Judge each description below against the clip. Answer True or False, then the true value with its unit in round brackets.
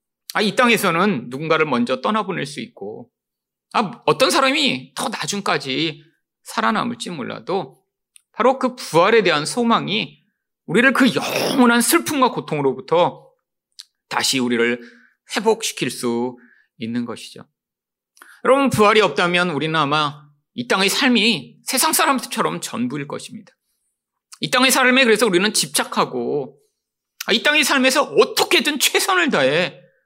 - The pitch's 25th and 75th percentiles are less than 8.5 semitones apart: False (8.9 semitones)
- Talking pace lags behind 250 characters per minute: False (285 characters per minute)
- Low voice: False (225 Hz)